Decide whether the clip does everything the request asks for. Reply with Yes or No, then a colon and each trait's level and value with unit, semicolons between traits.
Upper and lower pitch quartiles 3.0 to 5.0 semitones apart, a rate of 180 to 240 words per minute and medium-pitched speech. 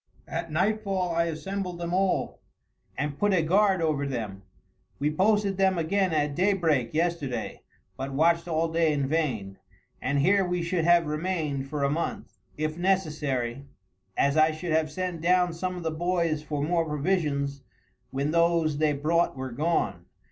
No: average, 3.4 semitones; average, 160 wpm; medium, 160 Hz